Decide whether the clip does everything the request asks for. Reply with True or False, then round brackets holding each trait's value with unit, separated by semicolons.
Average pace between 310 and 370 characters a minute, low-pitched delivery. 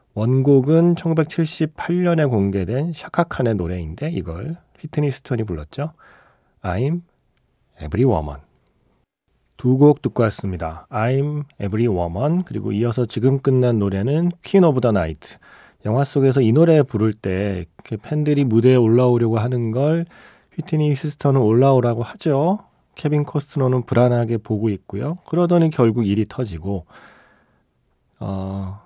True (315 characters per minute; 125 Hz)